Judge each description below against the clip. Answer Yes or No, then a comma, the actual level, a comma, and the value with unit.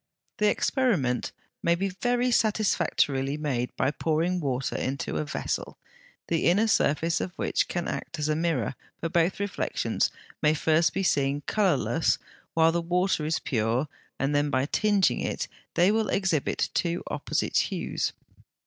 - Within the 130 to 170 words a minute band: Yes, average, 150 wpm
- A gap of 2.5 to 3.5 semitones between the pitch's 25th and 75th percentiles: No, average, 4.7 semitones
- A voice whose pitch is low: No, medium, 165 Hz